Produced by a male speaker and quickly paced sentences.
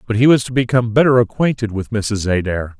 Yes: male; fast, 215 wpm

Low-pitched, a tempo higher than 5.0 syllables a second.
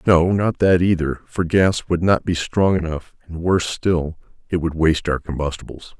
No: very low, 85 Hz; 4.8 syllables/s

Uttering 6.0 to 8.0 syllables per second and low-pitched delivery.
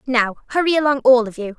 No: 6.5 syllables/s; very high, 255 Hz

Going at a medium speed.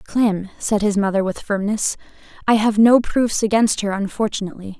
Yes: average, 165 wpm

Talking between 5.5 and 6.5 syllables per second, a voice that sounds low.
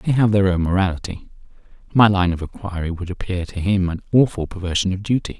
Yes: 6.1 syllables/s; very low, 95 Hz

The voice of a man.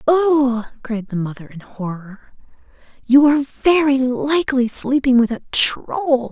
No: female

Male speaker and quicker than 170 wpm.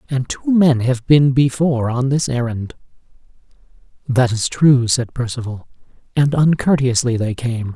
No: male; average, 140 wpm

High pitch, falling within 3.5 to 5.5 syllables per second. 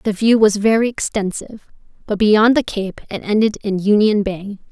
Yes: high, 210 Hz; 5.0 syllables/s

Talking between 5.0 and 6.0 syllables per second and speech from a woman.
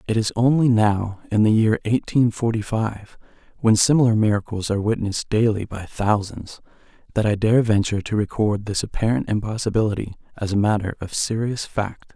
No: 5.4 syllables/s; male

